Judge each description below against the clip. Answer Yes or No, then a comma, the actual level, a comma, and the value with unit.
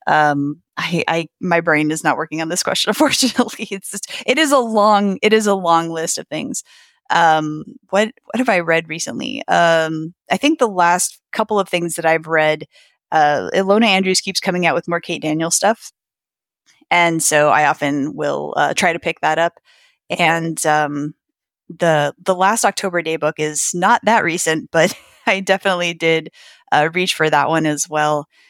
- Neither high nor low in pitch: Yes, medium, 170 Hz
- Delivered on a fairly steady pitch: No, average, 4.2 semitones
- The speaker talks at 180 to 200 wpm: Yes, average, 185 wpm